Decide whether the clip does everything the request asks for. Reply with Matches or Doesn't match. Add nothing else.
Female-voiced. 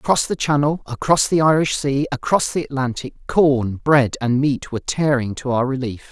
Doesn't match